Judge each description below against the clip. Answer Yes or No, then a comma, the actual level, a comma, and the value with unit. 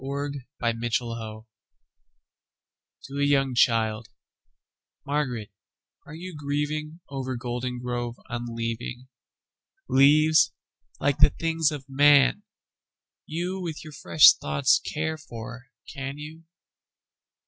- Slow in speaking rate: Yes, slow, 85 wpm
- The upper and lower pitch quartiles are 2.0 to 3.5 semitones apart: No, average, 4.0 semitones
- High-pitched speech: No, low, 135 Hz